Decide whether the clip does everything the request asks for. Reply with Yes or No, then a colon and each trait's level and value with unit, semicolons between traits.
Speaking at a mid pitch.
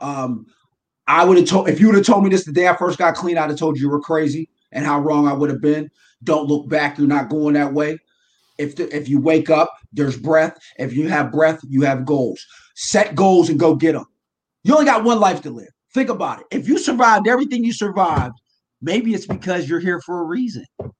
Yes: medium, 160 Hz